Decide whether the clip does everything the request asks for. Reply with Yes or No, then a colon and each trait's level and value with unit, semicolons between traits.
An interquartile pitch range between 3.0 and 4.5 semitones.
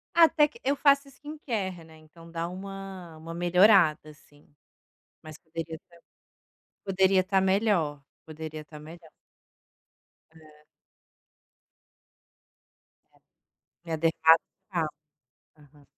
Yes: average, 3.6 semitones